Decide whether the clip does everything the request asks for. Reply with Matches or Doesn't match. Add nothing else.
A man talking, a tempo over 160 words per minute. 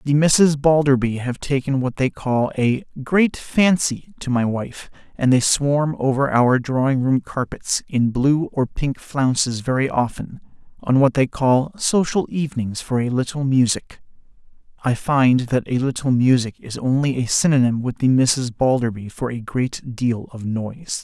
Matches